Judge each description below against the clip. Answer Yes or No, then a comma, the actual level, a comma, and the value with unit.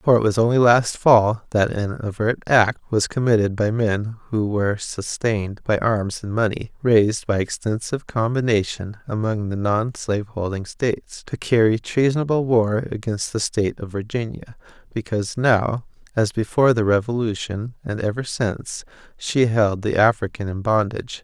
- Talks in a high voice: No, low, 110 Hz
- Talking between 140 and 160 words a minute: Yes, average, 155 wpm